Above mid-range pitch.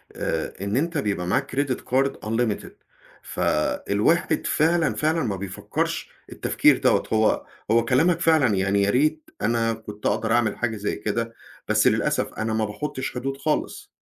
No: low, 115 Hz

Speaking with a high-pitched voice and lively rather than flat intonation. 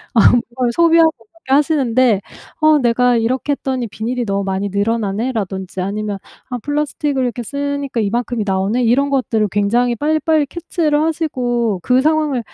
No: high, 245 Hz; average, 4.8 semitones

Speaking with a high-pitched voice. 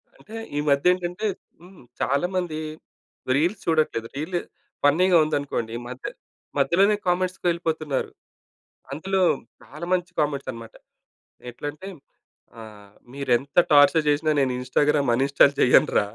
No: medium, 150 Hz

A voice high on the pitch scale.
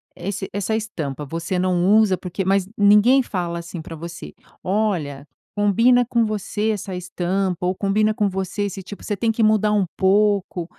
Yes: high, 195 Hz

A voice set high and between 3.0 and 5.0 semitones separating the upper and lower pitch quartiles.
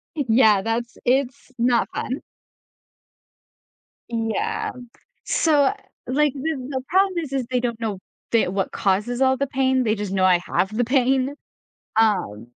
Yes: high, 245 Hz; average, 3.5 semitones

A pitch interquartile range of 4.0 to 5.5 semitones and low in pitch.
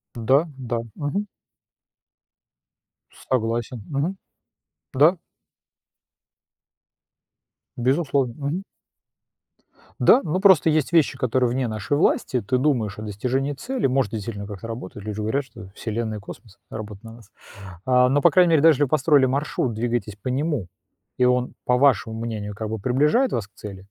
Yes: average, 4.6 semitones; low, 125 Hz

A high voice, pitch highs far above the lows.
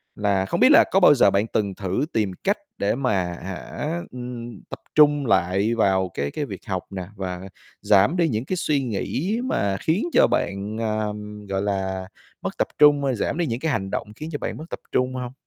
No: low, 110 Hz; wide, 7.1 semitones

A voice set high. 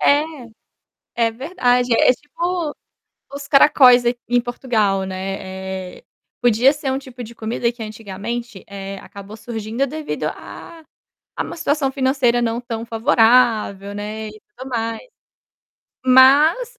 Yes: high, 240 Hz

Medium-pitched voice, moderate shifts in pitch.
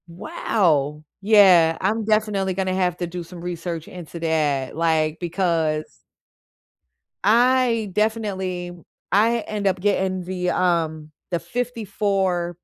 Yes: medium, 180 Hz; average, 3.6 semitones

